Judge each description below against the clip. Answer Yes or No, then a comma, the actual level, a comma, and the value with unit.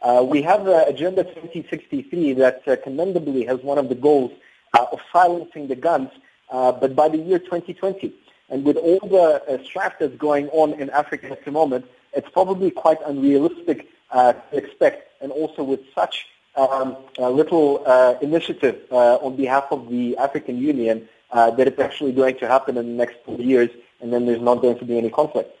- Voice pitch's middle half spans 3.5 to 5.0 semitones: Yes, average, 4.0 semitones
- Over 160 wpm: Yes, average, 195 wpm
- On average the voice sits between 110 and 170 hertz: Yes, medium, 140 Hz